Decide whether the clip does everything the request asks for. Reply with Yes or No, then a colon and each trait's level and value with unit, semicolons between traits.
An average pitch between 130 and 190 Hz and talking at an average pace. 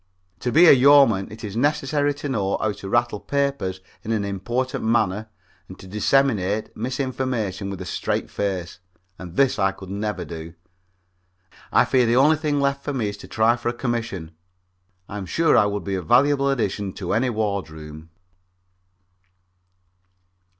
No: low, 110 Hz; average, 160 wpm